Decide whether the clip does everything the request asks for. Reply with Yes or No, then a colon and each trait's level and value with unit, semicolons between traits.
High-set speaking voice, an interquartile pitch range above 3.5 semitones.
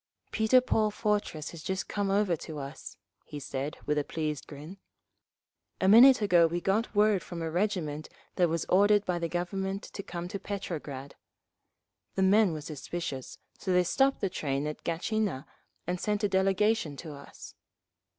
No: medium, 180 Hz; average, 4.8 semitones